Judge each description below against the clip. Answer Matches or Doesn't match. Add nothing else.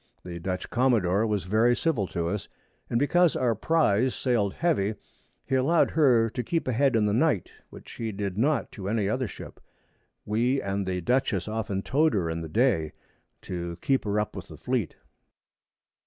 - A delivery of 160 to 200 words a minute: Matches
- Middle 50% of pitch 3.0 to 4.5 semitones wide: Doesn't match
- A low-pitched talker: Matches